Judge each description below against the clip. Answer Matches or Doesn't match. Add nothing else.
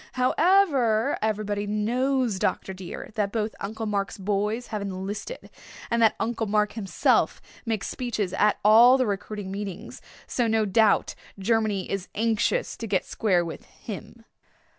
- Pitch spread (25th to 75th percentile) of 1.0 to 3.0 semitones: Matches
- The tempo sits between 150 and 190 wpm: Doesn't match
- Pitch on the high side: Matches